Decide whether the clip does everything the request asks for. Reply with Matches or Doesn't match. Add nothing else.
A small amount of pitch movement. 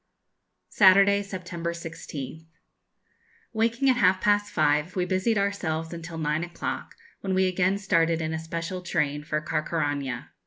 Doesn't match